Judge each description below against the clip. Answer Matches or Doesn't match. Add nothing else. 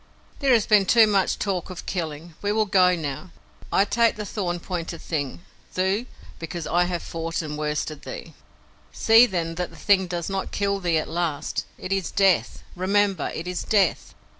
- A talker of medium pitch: Matches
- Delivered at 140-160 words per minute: Doesn't match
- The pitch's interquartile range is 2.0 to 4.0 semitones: Matches